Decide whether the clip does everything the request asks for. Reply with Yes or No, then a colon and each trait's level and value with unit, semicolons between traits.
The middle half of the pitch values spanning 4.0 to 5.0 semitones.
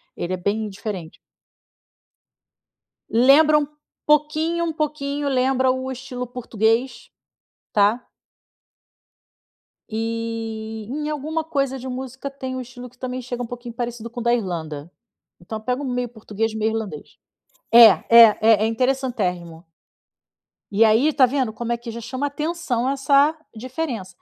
No: average, 3.4 semitones